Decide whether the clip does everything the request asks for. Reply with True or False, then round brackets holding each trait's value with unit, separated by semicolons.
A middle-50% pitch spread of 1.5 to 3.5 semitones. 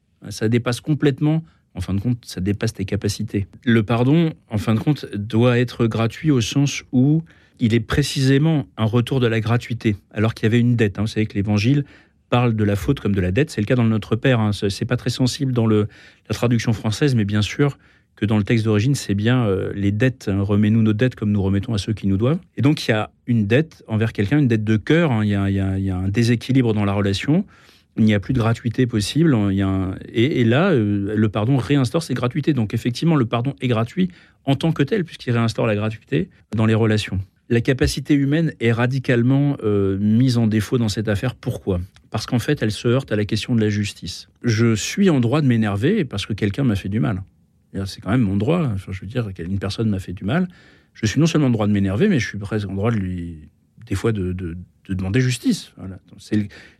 False (4.0 semitones)